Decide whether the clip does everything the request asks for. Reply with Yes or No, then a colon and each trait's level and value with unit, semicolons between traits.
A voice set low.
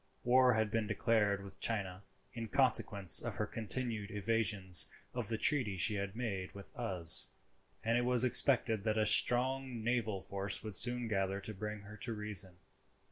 Yes: low, 110 Hz